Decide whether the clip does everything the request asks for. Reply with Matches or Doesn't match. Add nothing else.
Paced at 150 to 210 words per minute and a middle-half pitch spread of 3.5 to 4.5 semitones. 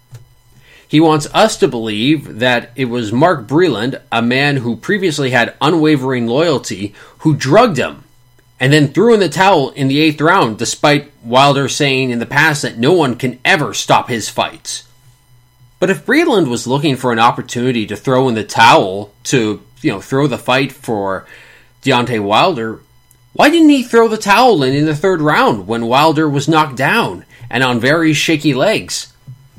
Matches